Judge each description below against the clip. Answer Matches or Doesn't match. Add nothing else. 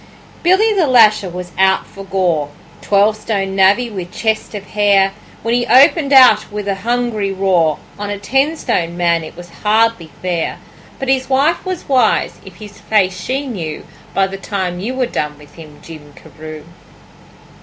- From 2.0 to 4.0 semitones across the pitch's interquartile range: Doesn't match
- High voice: Matches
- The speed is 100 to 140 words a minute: Doesn't match